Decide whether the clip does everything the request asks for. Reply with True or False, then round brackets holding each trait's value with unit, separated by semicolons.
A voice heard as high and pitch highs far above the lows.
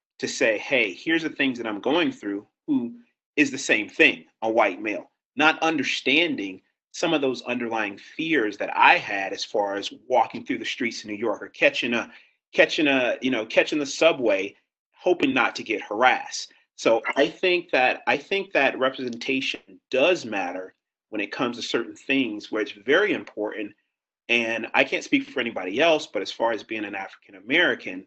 False (140 Hz; 8.8 semitones)